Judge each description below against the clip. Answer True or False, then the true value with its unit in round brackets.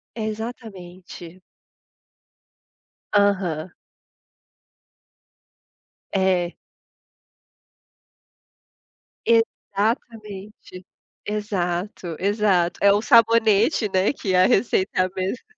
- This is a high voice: True (200 Hz)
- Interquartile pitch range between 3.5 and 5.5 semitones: False (2.9 semitones)